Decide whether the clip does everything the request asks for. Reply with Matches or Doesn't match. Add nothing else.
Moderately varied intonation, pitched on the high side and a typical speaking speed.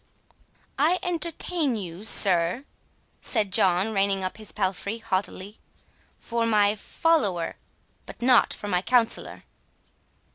Doesn't match